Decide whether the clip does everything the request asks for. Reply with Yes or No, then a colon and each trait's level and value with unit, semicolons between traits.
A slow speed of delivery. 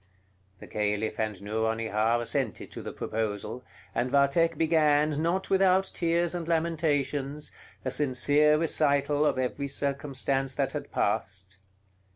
Yes: slow, 125 wpm